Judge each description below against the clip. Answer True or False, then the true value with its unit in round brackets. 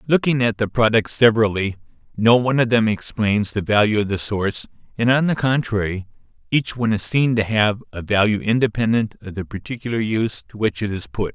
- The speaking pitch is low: True (110 Hz)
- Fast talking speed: False (195 wpm)